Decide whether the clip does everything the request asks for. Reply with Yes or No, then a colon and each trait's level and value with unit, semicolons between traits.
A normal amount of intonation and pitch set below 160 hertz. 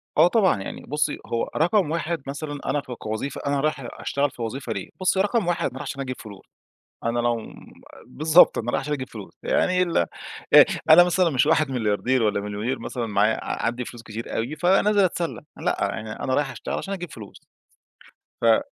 No: wide, 6.3 semitones; low, 135 Hz